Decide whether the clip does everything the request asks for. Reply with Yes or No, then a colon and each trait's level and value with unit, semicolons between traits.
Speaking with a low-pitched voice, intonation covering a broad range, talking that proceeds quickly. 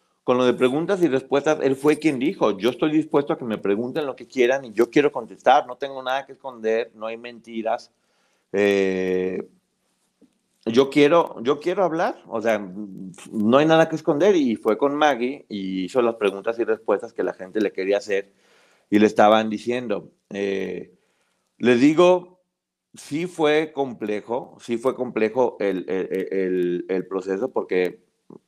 No: low, 120 Hz; wide, 6.1 semitones; average, 170 wpm